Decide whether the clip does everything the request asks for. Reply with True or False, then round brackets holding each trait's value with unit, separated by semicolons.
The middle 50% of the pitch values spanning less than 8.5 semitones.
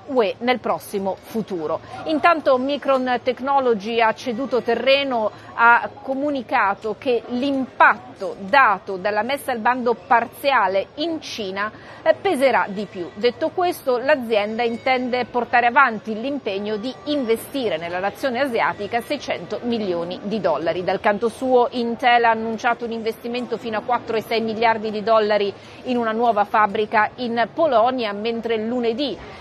True (3.2 semitones)